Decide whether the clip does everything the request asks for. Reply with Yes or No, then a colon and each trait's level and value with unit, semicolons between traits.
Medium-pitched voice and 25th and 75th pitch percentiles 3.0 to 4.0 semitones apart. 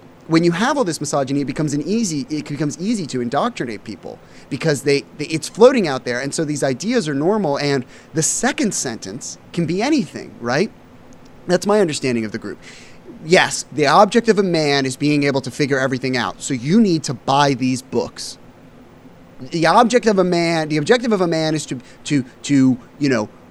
No: medium, 150 Hz; average, 4.4 semitones